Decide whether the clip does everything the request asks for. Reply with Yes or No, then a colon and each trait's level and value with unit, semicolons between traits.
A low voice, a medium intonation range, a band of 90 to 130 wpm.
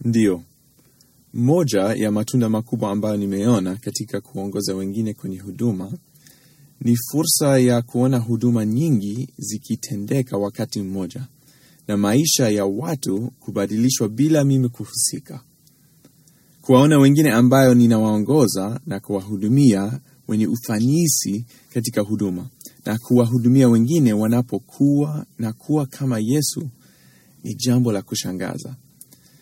Yes: low, 120 Hz; average, 4.6 semitones; average, 105 wpm